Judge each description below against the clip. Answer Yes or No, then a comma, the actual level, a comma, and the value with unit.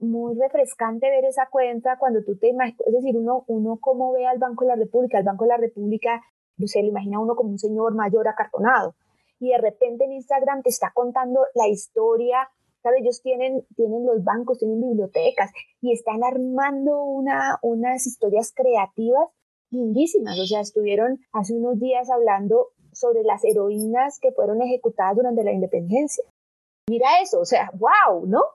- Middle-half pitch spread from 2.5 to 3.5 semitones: Yes, average, 2.8 semitones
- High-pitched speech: Yes, high, 245 Hz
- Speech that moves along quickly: No, average, 175 wpm